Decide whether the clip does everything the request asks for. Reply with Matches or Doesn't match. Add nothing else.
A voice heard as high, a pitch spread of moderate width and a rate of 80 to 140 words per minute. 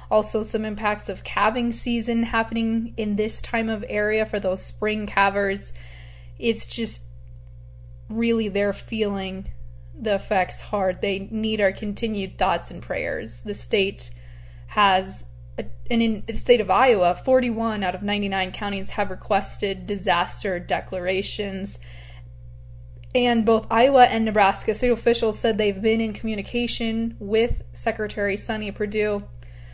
Matches